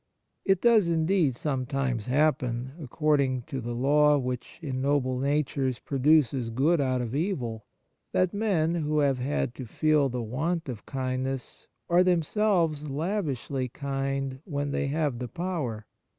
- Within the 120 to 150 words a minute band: Yes, average, 140 wpm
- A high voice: No, medium, 140 Hz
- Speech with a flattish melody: No, average, 3.6 semitones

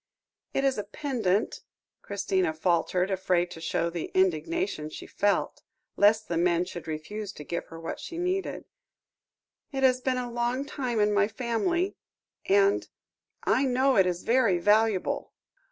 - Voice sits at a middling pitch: No, high, 210 Hz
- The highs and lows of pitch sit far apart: Yes, wide, 6.4 semitones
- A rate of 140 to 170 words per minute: Yes, average, 155 wpm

